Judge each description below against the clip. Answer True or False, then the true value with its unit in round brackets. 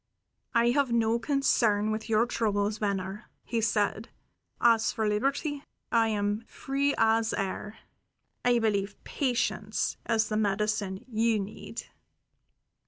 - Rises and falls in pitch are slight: True (2.2 semitones)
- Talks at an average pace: False (120 wpm)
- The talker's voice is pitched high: True (220 Hz)